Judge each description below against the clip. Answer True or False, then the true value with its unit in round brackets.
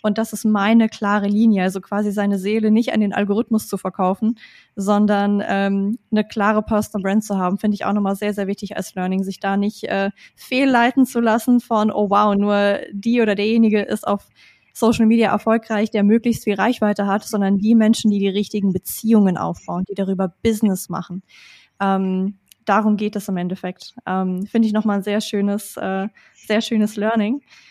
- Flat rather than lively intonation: True (2.0 semitones)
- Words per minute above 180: True (190 wpm)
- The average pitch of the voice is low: False (210 Hz)